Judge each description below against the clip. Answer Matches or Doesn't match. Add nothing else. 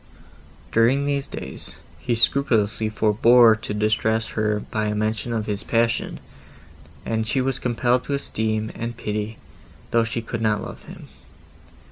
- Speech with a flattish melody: Matches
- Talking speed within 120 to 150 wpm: Matches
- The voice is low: Matches